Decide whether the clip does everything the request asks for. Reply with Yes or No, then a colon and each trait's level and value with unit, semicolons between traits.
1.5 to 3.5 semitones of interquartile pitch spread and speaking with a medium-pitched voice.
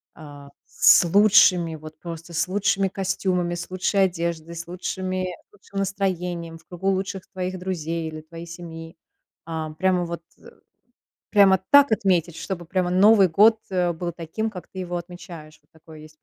Yes: narrow, 2.4 semitones; medium, 175 Hz